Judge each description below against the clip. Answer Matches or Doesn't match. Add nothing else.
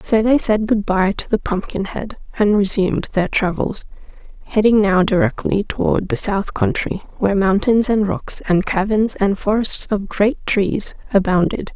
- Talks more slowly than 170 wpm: Matches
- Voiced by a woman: Matches